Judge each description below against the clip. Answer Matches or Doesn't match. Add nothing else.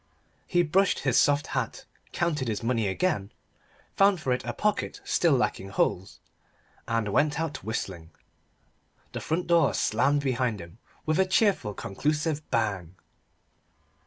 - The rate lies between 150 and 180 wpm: Doesn't match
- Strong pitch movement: Matches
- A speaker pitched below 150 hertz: Matches